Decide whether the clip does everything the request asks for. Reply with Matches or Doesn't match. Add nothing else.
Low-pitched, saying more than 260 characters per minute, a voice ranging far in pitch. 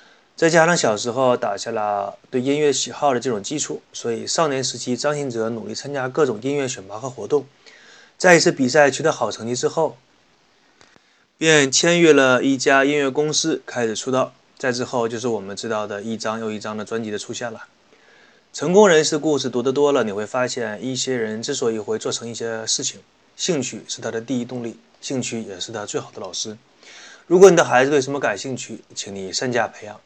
Doesn't match